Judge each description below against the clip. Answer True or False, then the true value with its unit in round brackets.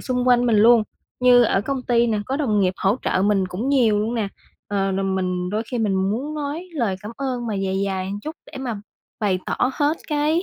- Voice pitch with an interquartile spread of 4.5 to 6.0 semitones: True (4.8 semitones)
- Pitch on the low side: False (225 Hz)